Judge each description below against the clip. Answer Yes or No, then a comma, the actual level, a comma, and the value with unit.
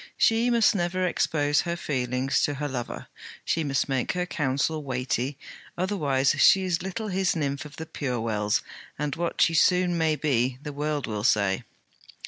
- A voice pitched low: No, medium, 150 Hz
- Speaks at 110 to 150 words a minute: No, average, 170 wpm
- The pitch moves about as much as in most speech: Yes, average, 4.8 semitones